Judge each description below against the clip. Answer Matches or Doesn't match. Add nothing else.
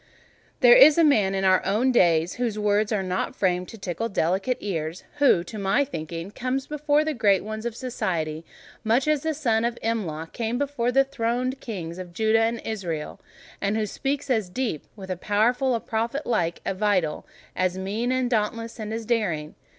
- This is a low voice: Doesn't match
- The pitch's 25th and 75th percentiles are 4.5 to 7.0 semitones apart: Matches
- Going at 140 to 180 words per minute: Doesn't match